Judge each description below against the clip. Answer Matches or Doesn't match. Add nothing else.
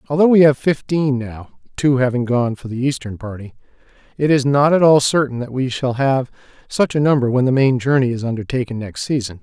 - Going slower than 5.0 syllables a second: Matches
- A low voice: Matches